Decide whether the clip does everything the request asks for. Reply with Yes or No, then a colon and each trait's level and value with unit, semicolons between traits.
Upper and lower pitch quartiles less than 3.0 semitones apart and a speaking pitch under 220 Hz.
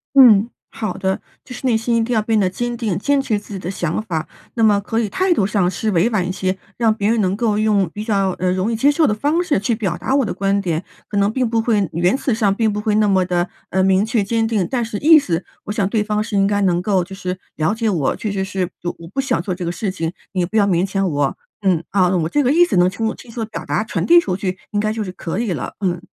No: average, 3.4 semitones; high, 205 Hz